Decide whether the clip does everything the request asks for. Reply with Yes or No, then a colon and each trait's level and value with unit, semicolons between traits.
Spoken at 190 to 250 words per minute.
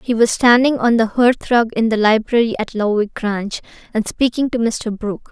Yes: fast, 205 wpm